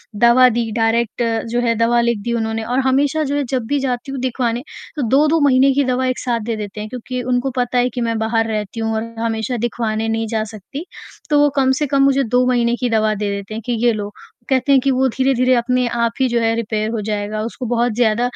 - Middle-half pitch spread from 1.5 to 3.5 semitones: Yes, narrow, 2.5 semitones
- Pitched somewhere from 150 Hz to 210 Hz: No, high, 240 Hz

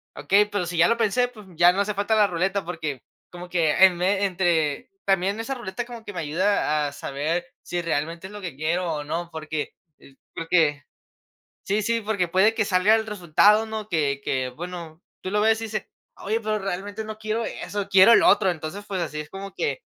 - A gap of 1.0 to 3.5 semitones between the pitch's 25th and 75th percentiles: No, average, 4.1 semitones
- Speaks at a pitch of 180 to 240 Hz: Yes, medium, 185 Hz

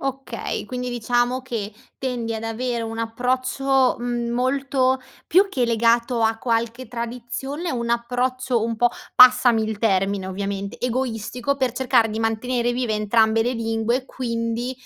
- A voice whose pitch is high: Yes, high, 240 Hz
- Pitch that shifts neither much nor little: No, narrow, 2.1 semitones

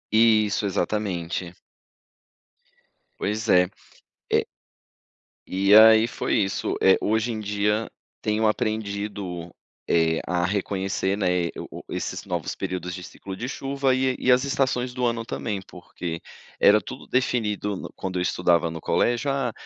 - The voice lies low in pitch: Yes, low, 105 Hz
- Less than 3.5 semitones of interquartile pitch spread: No, average, 3.9 semitones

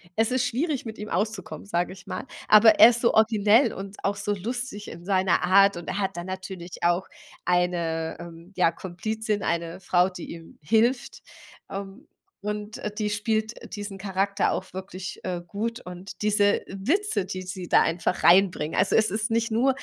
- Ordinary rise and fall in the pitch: Yes, average, 3.4 semitones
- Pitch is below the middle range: No, high, 200 Hz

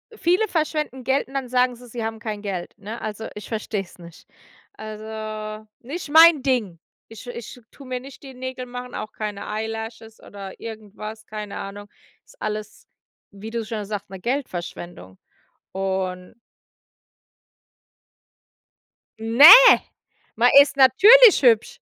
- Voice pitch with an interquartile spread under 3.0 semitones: No, average, 3.5 semitones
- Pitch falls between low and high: No, high, 220 Hz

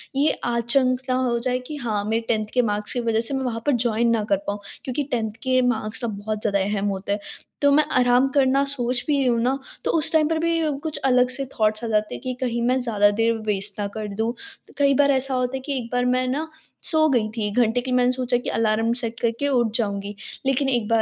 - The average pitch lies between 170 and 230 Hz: No, high, 245 Hz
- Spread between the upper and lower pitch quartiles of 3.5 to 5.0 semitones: No, average, 3.1 semitones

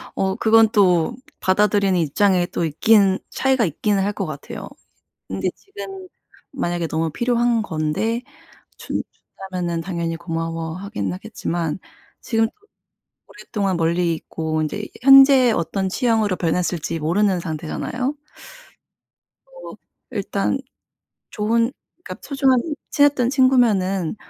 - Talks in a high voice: Yes, high, 195 Hz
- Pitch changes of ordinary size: No, wide, 5.8 semitones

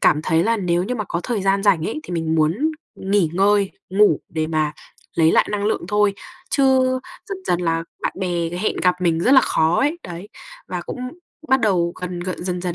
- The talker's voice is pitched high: No, medium, 180 Hz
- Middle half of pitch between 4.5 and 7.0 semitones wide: No, average, 3.8 semitones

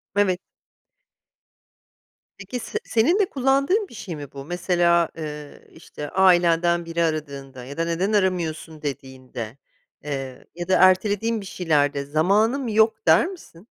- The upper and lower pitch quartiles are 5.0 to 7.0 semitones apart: Yes, wide, 5.6 semitones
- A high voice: No, medium, 175 Hz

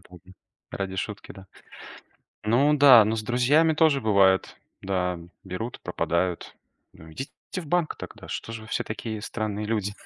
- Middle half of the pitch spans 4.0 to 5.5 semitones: Yes, average, 4.8 semitones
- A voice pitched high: No, low, 110 Hz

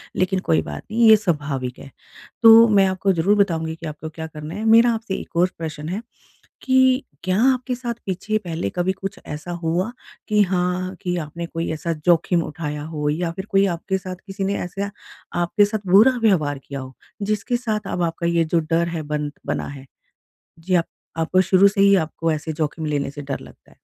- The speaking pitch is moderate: Yes, medium, 175 Hz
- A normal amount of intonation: Yes, average, 4.0 semitones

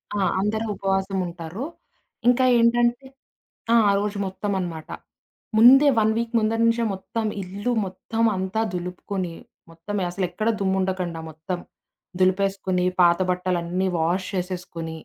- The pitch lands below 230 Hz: Yes, high, 190 Hz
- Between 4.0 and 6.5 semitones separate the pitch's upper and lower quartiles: No, average, 3.3 semitones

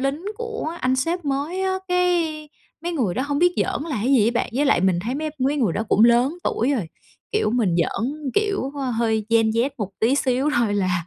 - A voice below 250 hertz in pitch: No, very high, 270 Hz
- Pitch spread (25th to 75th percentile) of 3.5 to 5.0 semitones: No, wide, 5.5 semitones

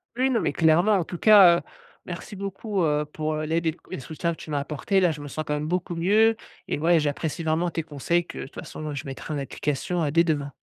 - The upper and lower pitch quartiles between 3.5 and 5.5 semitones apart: No, average, 3.1 semitones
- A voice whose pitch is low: No, medium, 160 Hz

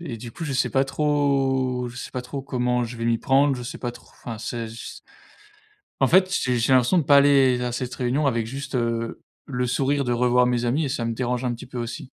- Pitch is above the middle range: No, low, 125 Hz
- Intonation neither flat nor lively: No, narrow, 2.2 semitones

